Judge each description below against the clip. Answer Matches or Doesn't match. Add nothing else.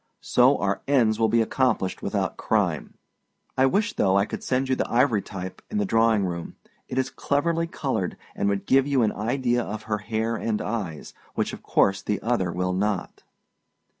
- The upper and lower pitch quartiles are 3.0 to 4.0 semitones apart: Doesn't match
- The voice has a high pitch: Doesn't match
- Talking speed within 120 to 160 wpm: Doesn't match